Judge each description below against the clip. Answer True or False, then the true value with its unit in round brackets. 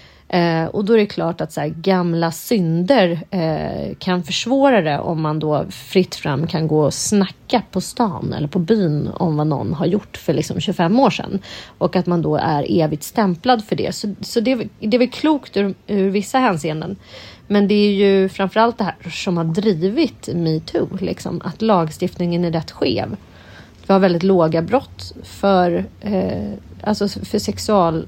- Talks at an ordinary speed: True (185 wpm)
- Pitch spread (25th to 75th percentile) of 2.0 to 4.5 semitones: True (3.9 semitones)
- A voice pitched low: False (185 Hz)